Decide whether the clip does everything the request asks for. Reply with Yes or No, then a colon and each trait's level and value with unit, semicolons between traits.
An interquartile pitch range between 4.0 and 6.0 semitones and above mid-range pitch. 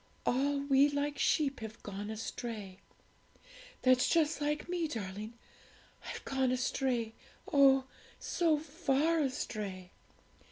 Yes: average, 4.8 semitones; very high, 265 Hz